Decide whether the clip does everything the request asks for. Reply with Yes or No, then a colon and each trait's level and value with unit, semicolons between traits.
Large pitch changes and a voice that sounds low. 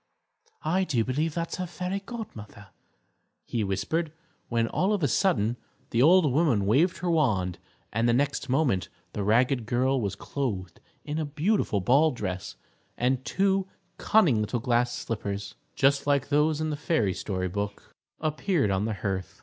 Yes: wide, 7.0 semitones; low, 130 Hz